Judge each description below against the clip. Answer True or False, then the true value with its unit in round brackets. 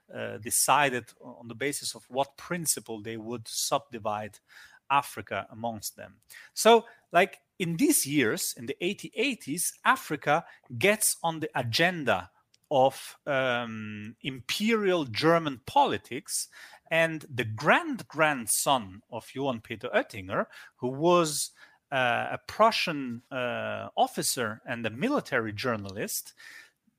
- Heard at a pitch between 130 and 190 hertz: True (140 Hz)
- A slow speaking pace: True (115 wpm)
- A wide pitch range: True (6.4 semitones)